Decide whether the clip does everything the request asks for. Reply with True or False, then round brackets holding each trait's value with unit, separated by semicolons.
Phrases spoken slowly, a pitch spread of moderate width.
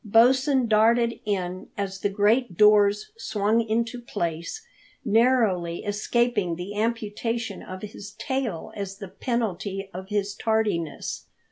True (120 wpm; 3.0 semitones)